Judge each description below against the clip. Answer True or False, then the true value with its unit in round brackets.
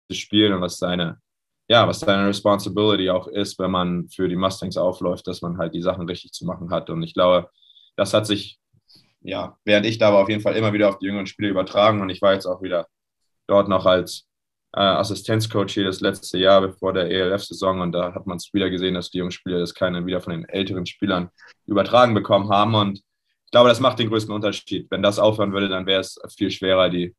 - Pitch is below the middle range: True (95 Hz)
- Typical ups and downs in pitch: False (2.0 semitones)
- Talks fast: True (225 wpm)